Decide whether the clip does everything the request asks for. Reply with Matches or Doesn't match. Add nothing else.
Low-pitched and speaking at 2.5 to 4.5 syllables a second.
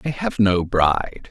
Matches